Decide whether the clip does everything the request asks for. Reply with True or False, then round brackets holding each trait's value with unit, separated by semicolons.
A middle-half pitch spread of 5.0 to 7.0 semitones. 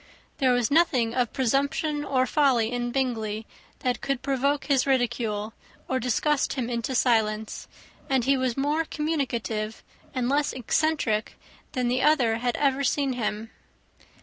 False (3.2 semitones)